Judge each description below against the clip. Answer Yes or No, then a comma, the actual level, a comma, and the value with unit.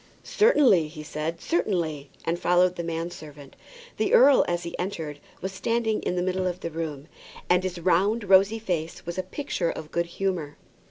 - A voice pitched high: No, medium, 175 Hz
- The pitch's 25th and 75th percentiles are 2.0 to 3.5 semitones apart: Yes, average, 2.9 semitones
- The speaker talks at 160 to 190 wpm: Yes, average, 180 wpm